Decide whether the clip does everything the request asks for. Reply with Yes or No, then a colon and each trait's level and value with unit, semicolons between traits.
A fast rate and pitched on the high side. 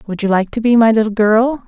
Yes: fast, 285 wpm; high, 220 Hz